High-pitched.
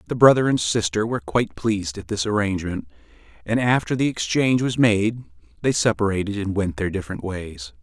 No: low, 105 Hz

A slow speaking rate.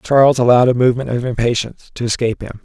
No: fast, 205 wpm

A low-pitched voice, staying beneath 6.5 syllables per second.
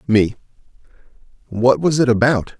Yes: low, 120 Hz; 4.6 syllables/s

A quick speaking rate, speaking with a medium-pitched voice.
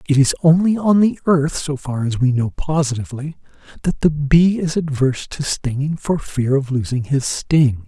No: average, 190 wpm; medium, 145 Hz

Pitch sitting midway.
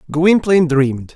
Yes: medium, 160 Hz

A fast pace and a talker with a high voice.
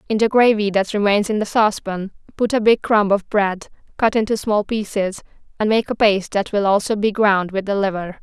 Yes: fast, 220 wpm; high, 205 Hz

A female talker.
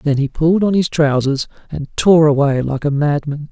No: male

